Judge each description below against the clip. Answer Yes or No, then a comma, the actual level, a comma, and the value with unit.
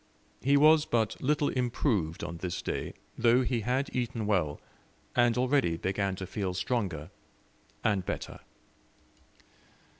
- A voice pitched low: Yes, low, 115 Hz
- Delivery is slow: Yes, slow, 125 wpm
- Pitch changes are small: No, average, 5.3 semitones